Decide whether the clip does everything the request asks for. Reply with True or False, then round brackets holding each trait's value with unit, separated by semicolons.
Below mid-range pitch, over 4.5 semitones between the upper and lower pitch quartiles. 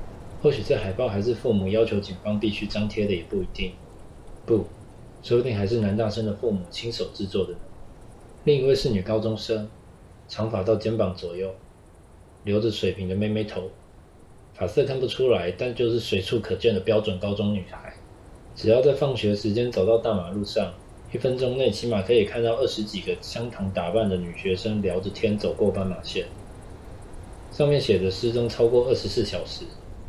False (105 Hz; 3.4 semitones)